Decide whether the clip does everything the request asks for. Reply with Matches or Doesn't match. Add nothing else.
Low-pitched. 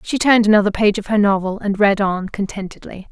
Doesn't match